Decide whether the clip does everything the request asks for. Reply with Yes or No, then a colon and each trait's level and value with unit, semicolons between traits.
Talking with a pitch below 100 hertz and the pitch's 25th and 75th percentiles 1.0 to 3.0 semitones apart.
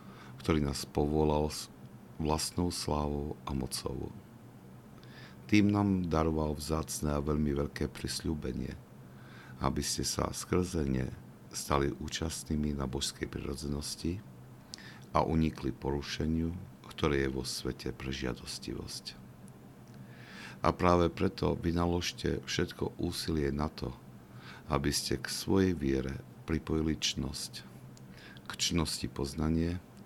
No: very low, 75 Hz; average, 3.4 semitones